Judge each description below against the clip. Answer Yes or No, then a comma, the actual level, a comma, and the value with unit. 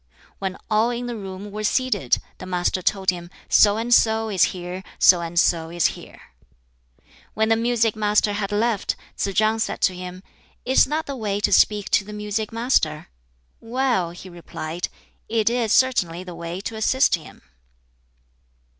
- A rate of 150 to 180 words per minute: Yes, average, 170 wpm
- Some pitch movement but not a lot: Yes, average, 3.9 semitones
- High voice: Yes, high, 205 Hz